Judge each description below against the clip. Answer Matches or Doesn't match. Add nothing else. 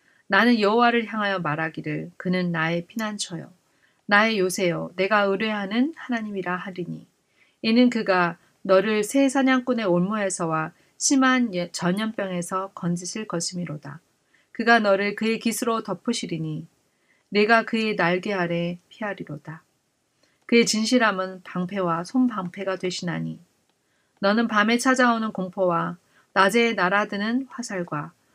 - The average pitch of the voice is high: Matches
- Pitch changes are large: Doesn't match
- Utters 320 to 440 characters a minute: Doesn't match